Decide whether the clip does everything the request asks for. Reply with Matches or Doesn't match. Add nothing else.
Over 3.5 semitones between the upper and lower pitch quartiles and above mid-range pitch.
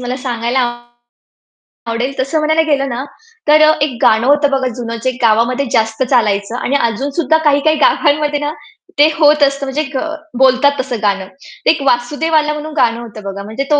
Matches